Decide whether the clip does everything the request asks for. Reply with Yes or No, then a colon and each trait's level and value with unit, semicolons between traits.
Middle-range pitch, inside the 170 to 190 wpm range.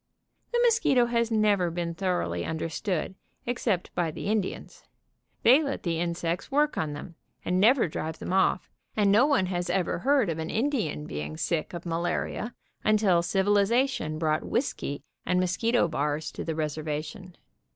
No: medium, 180 Hz; average, 155 wpm